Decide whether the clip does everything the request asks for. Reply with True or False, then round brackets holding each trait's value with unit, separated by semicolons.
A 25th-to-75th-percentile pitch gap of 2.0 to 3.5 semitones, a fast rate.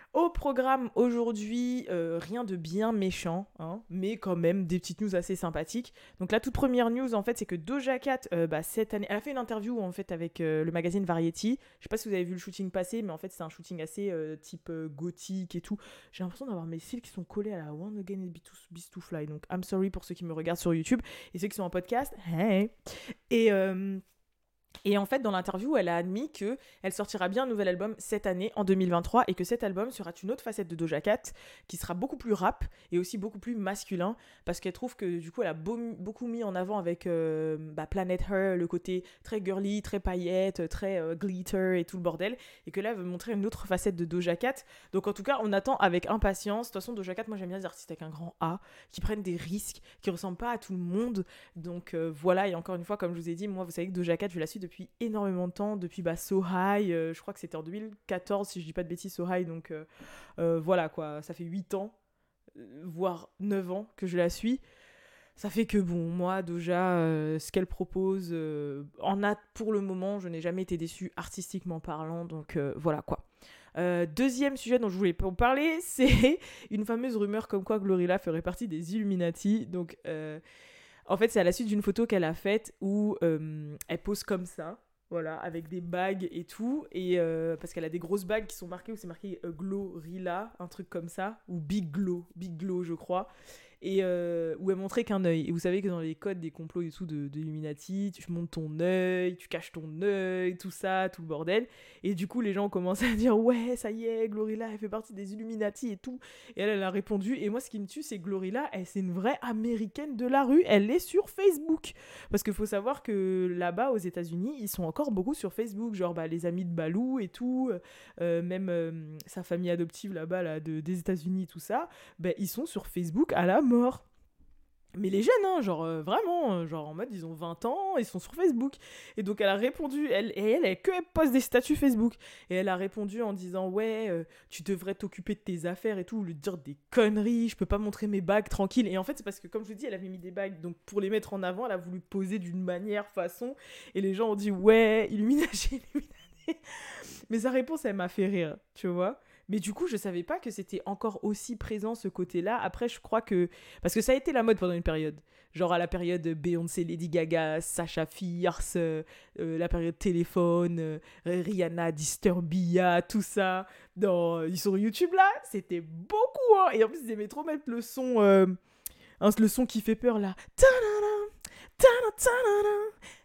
False (4.1 semitones; 235 wpm)